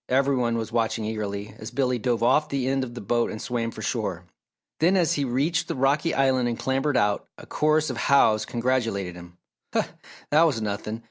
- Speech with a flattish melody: No, average, 3.8 semitones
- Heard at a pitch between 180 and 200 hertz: No, low, 125 Hz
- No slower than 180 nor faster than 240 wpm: Yes, fast, 205 wpm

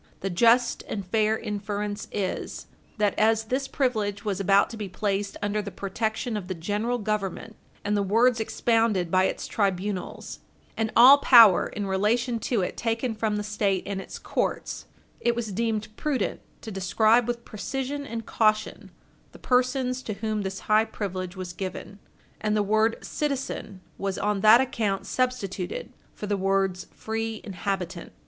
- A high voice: Yes, high, 215 Hz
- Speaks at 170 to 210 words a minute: No, average, 160 wpm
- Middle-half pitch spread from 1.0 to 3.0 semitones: Yes, average, 2.7 semitones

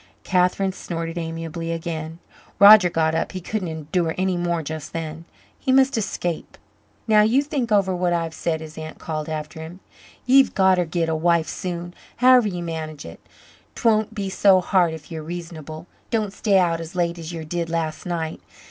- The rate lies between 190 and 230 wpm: No, average, 180 wpm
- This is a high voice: No, medium, 170 Hz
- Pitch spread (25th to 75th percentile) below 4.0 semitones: Yes, average, 2.9 semitones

